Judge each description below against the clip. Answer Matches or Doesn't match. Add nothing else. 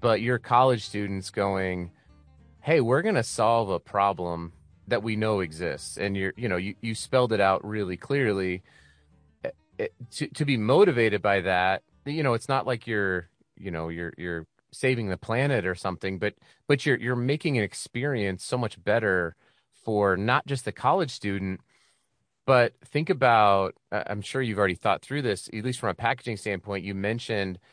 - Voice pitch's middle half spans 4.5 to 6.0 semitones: Matches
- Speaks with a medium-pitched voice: Doesn't match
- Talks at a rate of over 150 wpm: Matches